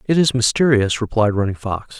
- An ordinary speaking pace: Yes, average, 180 wpm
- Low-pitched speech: Yes, low, 120 Hz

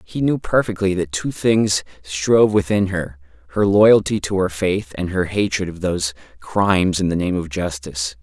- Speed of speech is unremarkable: Yes, average, 180 wpm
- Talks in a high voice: No, very low, 95 Hz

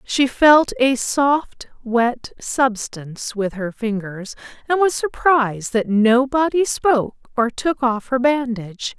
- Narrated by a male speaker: No, female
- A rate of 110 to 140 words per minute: Yes, slow, 135 wpm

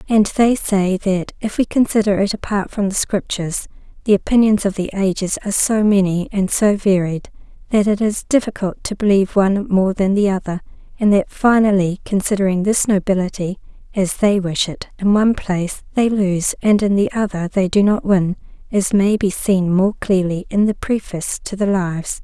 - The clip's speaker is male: No, female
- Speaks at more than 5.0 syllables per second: Yes, 5.2 syllables/s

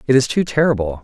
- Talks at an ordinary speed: No, fast, 230 wpm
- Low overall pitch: Yes, low, 125 Hz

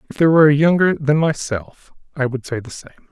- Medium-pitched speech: Yes, medium, 145 Hz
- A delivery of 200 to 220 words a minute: No, fast, 230 wpm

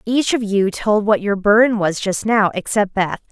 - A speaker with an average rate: No, fast, 215 wpm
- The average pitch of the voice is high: Yes, high, 210 Hz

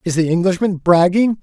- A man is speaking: Yes, male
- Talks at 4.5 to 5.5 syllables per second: Yes, 5.3 syllables/s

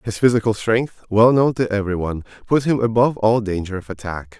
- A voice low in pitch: Yes, low, 110 Hz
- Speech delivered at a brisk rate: No, average, 190 wpm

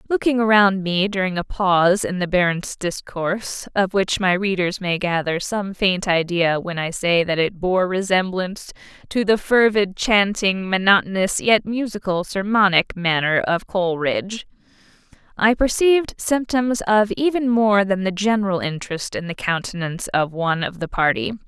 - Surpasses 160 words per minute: No, average, 155 wpm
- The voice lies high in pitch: Yes, high, 195 Hz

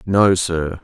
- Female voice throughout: No, male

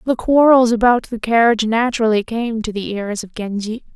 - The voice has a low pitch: No, high, 225 Hz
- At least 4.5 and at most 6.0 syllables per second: Yes, 5.4 syllables/s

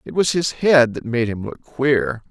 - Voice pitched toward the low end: Yes, low, 130 Hz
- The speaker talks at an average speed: No, fast, 235 wpm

